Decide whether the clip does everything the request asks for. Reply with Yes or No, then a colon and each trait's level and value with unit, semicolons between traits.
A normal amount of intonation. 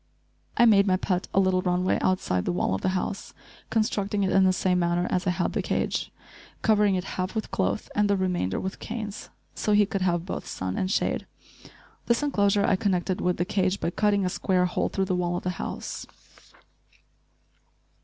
No: narrow, 2.0 semitones